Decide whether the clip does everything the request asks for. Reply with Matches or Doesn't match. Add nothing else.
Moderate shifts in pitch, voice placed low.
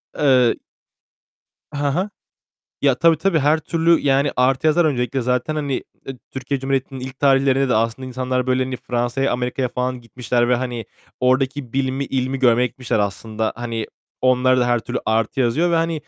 Doesn't match